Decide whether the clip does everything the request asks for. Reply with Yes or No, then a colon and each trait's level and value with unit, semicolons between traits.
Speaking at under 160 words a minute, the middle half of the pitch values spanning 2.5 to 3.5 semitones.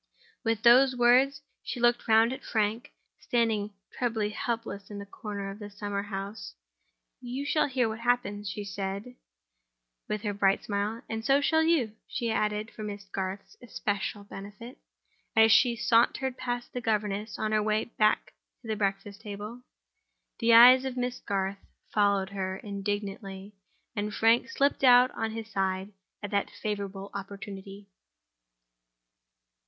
Yes: average, 150 wpm; average, 3.0 semitones